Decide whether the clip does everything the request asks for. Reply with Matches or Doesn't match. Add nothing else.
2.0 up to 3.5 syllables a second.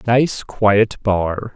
Matches